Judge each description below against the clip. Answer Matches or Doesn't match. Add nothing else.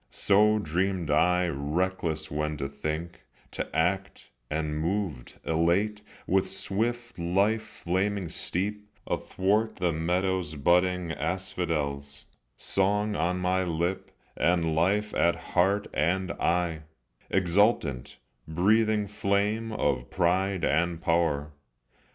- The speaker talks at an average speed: Doesn't match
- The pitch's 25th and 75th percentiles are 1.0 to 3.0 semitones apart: Doesn't match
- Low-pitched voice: Matches